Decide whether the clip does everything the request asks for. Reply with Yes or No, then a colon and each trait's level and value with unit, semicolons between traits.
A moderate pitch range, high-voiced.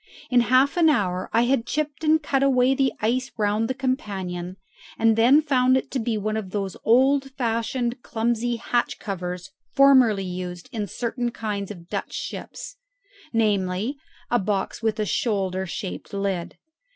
Yes: average, 4.6 semitones; high, 225 Hz